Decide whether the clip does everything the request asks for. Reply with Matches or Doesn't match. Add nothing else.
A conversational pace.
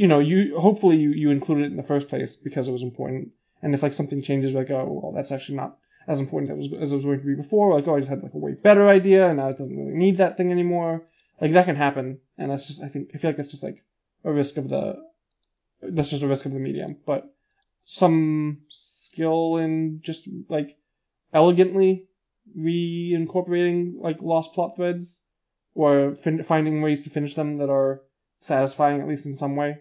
Doesn't match